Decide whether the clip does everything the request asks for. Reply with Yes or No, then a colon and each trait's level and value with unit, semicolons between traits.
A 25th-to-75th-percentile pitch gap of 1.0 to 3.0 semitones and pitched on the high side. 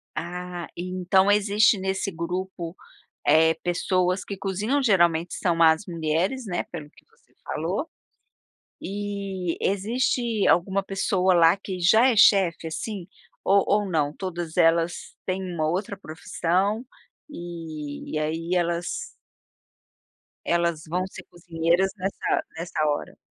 No: average, 2.7 semitones; medium, 180 Hz